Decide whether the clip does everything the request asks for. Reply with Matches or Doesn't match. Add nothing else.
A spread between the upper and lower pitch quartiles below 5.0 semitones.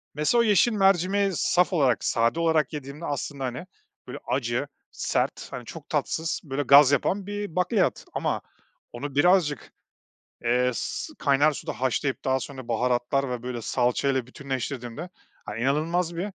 Doesn't match